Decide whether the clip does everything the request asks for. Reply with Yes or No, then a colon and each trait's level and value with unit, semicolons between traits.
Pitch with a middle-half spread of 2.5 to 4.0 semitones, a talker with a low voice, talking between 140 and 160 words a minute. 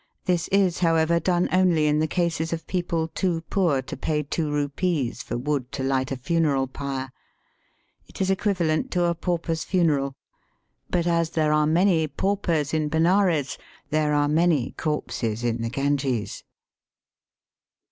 No: average, 3.5 semitones; medium, 160 Hz; average, 150 wpm